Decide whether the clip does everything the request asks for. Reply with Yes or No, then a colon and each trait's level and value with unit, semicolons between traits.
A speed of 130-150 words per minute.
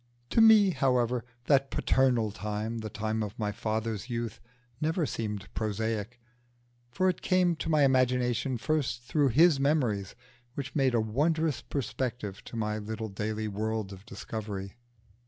Yes: average, 145 wpm